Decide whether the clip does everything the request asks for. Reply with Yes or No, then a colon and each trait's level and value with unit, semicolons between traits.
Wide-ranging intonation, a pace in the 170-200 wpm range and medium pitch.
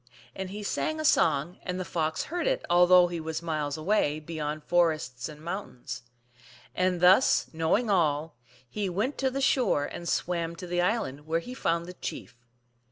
No: average, 3.7 semitones; average, 180 wpm; medium, 175 Hz